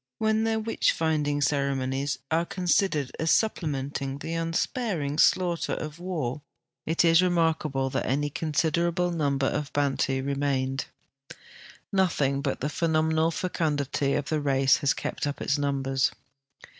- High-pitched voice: No, medium, 150 Hz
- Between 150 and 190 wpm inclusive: No, slow, 135 wpm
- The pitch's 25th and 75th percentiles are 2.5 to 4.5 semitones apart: Yes, average, 3.2 semitones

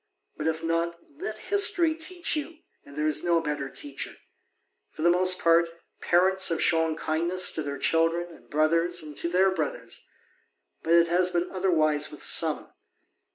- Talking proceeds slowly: No, average, 160 wpm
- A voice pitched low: No, medium, 170 Hz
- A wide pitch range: No, narrow, 2.5 semitones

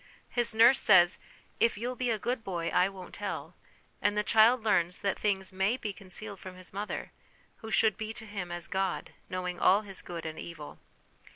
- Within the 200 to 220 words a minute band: Yes, fast, 205 wpm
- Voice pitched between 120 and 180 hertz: No, high, 195 Hz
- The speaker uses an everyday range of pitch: Yes, average, 3.3 semitones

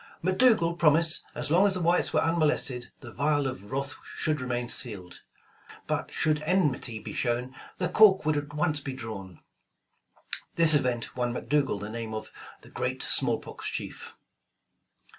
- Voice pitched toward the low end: No, medium, 145 Hz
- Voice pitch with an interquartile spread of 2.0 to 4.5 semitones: No, average, 5.2 semitones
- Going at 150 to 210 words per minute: Yes, average, 160 wpm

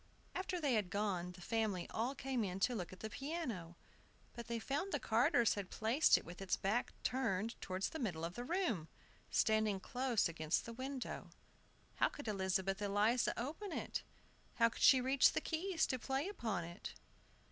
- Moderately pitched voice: No, high, 225 Hz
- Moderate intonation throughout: No, wide, 5.7 semitones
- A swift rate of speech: No, average, 180 wpm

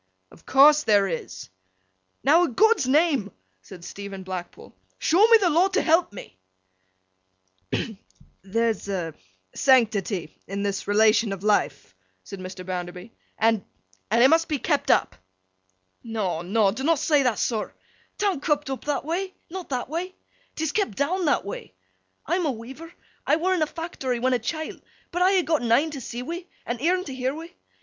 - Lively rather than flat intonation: Yes, wide, 8.3 semitones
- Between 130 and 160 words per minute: No, average, 170 wpm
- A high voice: Yes, very high, 255 Hz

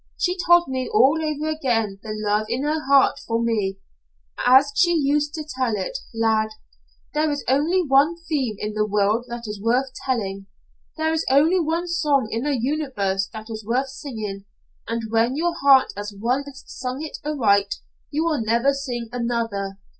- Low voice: No, very high, 255 Hz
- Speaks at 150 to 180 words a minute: Yes, average, 175 wpm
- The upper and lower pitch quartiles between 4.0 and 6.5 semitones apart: Yes, average, 5.3 semitones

